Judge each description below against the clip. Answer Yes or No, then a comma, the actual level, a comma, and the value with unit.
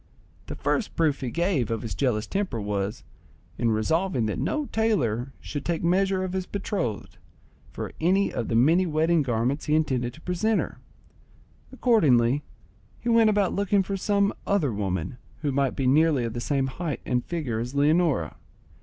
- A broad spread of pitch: Yes, wide, 7.6 semitones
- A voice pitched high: No, medium, 150 Hz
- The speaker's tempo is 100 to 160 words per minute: No, average, 170 wpm